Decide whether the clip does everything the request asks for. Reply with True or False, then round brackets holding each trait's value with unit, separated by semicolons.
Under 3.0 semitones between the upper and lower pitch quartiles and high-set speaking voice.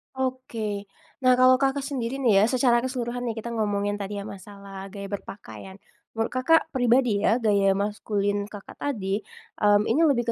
False (4.0 semitones; 220 Hz)